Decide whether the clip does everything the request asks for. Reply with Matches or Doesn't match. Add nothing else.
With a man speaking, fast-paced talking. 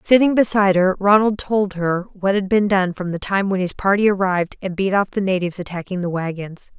Doesn't match